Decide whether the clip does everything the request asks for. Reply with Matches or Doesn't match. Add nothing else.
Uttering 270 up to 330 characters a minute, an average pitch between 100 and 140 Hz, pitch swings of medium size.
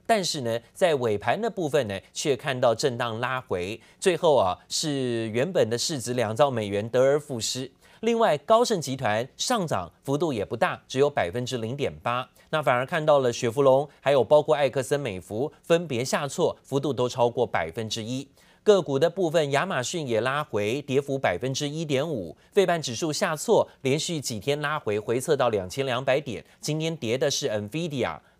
Matches